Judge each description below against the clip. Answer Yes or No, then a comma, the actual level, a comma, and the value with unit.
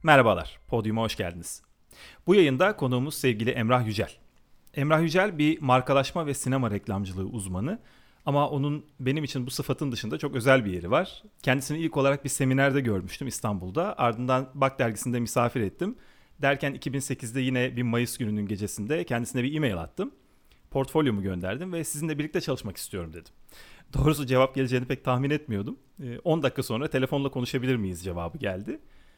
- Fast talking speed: Yes, fast, 155 wpm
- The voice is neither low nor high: No, low, 130 Hz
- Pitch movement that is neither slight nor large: Yes, average, 4.0 semitones